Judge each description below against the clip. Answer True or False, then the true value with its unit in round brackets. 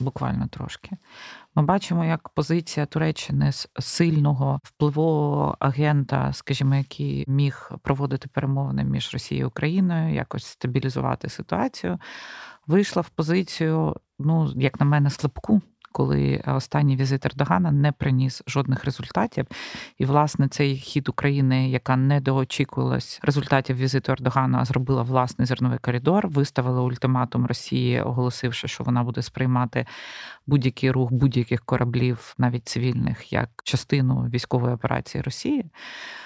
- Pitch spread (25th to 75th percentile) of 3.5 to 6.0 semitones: False (2.8 semitones)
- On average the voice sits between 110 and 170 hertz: True (135 Hz)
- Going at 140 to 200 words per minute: False (120 wpm)